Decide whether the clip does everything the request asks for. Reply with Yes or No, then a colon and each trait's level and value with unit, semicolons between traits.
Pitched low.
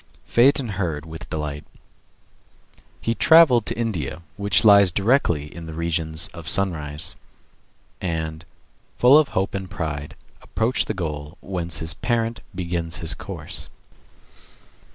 Yes: very low, 85 Hz